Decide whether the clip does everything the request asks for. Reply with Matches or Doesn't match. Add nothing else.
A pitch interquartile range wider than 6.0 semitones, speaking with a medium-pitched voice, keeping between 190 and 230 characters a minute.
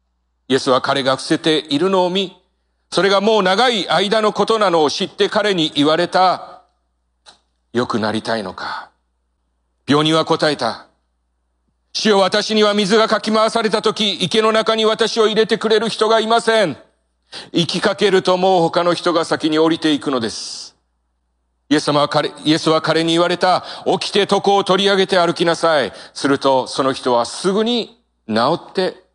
Doesn't match